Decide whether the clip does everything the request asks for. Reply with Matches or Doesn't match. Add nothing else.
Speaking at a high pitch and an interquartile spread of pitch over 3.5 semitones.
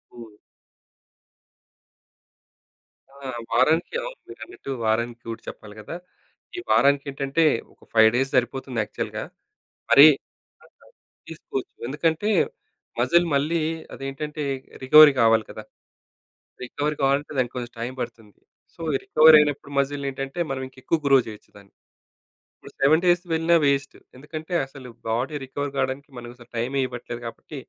Doesn't match